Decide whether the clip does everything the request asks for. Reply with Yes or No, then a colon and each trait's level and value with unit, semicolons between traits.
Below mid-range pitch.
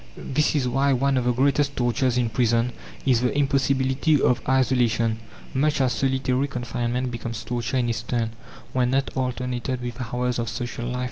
Yes: low, 125 Hz